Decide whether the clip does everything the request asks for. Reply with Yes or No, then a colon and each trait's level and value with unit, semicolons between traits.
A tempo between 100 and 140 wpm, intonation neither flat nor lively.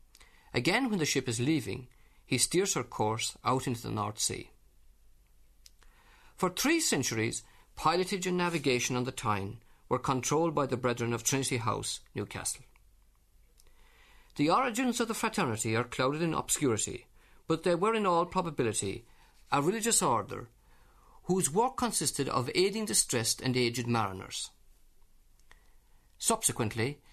No: slow, 135 wpm; wide, 8.0 semitones